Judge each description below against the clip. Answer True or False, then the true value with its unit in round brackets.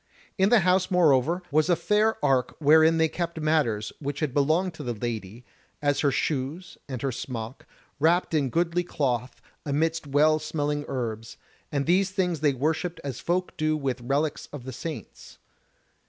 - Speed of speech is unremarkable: True (170 wpm)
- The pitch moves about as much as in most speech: True (4.1 semitones)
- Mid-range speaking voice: True (150 Hz)